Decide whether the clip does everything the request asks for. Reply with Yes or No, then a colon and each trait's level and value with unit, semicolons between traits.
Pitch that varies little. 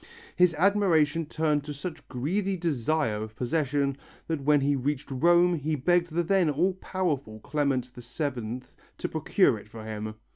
No: average, 4.6 semitones